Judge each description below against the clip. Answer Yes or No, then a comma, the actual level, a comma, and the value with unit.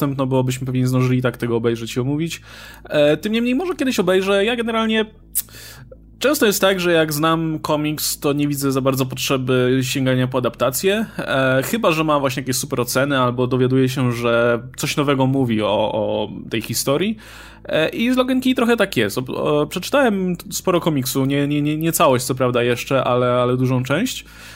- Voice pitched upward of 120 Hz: Yes, medium, 140 Hz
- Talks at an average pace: No, fast, 190 wpm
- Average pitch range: No, wide, 6.2 semitones